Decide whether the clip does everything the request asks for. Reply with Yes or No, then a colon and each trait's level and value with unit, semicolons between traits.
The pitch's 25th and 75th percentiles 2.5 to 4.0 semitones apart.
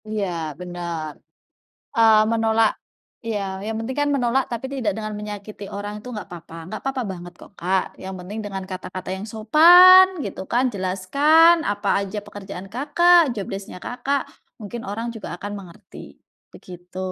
No: average, 4.5 semitones